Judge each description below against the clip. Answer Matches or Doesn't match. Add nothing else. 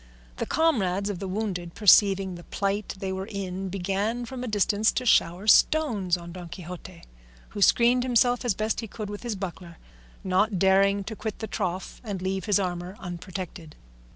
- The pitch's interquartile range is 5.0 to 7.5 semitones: Doesn't match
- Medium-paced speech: Matches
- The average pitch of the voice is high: Matches